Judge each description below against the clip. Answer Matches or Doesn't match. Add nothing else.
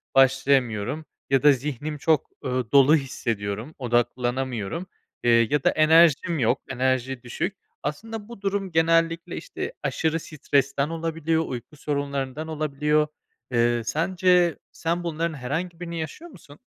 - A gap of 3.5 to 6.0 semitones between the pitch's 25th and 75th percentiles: Matches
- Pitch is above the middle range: Doesn't match